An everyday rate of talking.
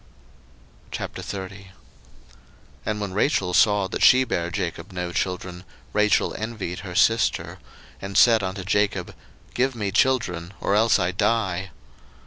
No: slow, 125 wpm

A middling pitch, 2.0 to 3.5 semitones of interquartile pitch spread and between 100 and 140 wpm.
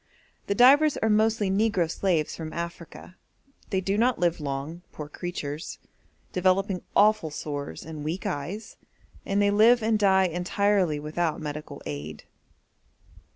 No: medium, 180 Hz; average, 5.1 semitones; slow, 135 wpm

